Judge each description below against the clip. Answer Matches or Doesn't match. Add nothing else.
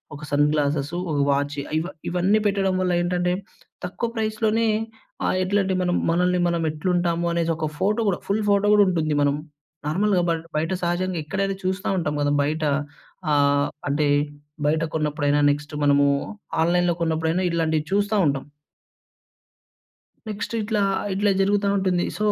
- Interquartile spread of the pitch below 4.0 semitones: Doesn't match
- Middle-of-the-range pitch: Matches